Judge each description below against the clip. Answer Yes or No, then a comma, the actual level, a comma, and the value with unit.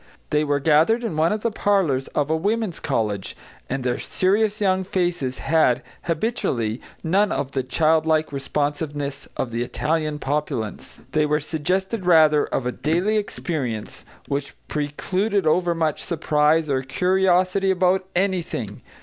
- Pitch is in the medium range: Yes, medium, 160 Hz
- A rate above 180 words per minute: No, average, 140 wpm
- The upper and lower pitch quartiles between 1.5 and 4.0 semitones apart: No, average, 4.6 semitones